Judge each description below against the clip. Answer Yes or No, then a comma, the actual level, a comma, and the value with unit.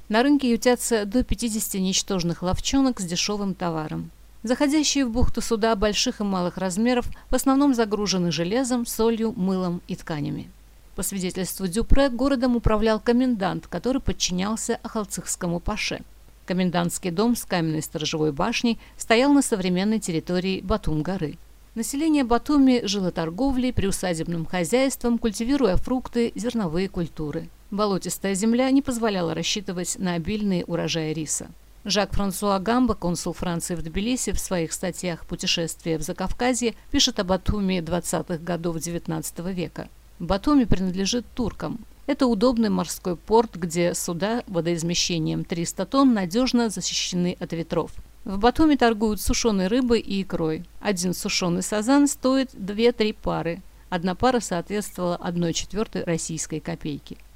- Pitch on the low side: No, high, 195 Hz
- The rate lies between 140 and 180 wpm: No, average, 130 wpm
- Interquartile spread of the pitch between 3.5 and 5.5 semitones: Yes, average, 5.2 semitones